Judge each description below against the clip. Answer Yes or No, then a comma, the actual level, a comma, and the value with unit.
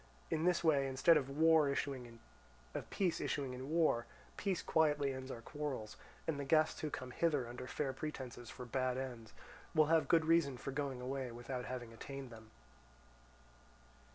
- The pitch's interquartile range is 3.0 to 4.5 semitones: Yes, average, 3.8 semitones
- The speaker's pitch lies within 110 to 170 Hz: Yes, low, 135 Hz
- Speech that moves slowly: No, average, 155 wpm